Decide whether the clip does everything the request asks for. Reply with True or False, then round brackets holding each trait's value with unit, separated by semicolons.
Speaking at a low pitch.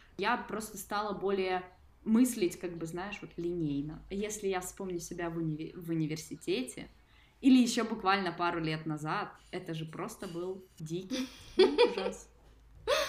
False (185 Hz)